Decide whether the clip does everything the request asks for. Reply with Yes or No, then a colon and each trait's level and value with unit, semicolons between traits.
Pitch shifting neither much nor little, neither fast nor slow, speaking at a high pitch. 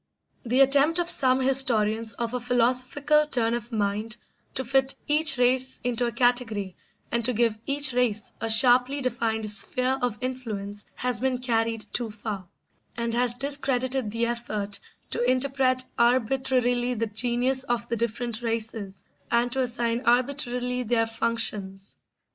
No: narrow, 2.2 semitones; average, 145 wpm; high, 240 Hz